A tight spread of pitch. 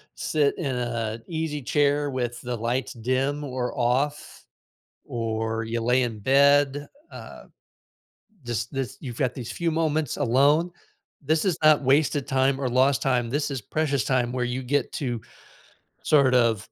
No: average, 3.1 semitones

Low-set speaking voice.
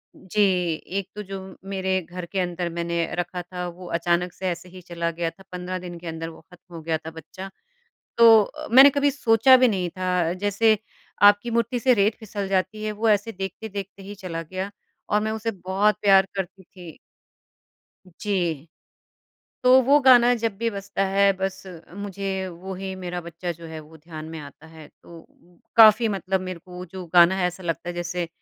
No: high, 190 Hz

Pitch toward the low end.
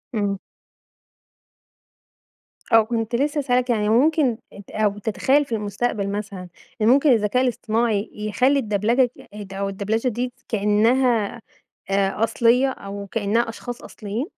No: high, 225 Hz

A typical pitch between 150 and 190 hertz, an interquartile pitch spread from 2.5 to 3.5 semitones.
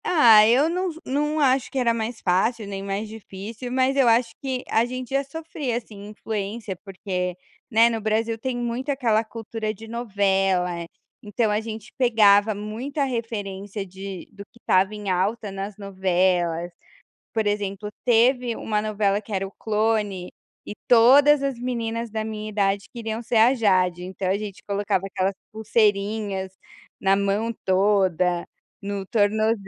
No: high, 215 Hz; average, 3.1 semitones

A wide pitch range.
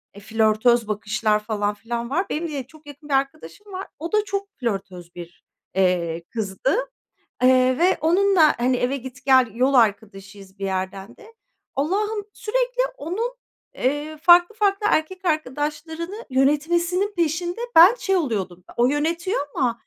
Yes: wide, 8.1 semitones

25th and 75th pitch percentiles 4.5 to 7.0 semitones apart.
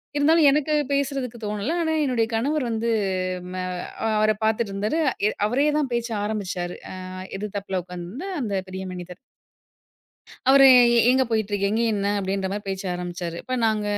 Yes: average, 5.1 semitones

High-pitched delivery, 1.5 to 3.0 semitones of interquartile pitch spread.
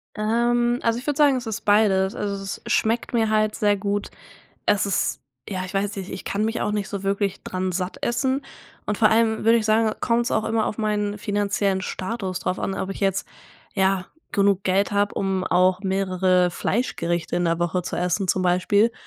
Yes: high, 200 Hz; narrow, 2.6 semitones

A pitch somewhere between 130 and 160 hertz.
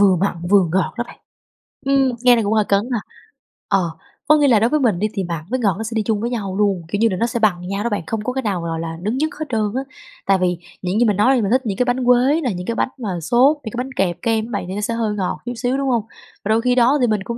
No: high, 220 Hz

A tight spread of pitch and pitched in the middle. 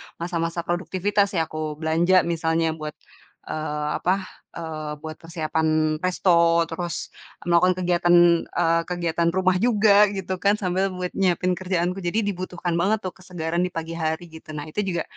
Yes: narrow, 2.2 semitones; medium, 175 Hz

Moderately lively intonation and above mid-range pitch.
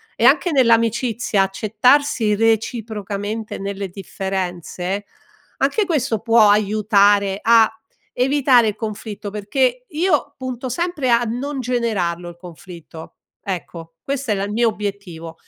Yes: average, 4.1 semitones; high, 220 Hz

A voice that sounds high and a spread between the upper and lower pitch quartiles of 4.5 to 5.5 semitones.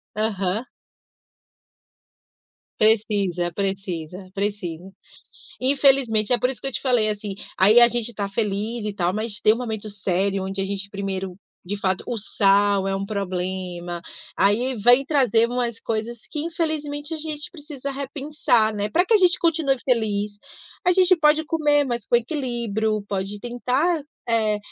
Yes: high, 220 Hz; average, 5.2 semitones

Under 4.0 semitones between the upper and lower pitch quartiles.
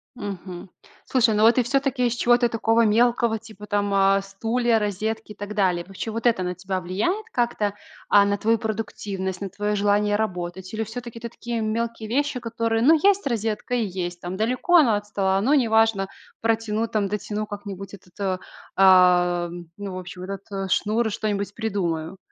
Yes: average, 2.9 semitones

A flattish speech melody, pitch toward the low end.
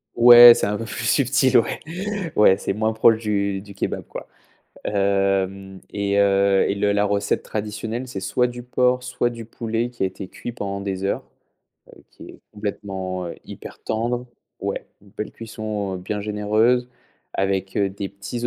No: average, 3.0 semitones; low, 105 Hz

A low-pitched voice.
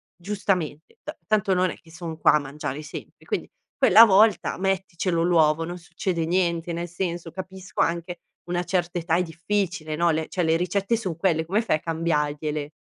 No: medium, 175 Hz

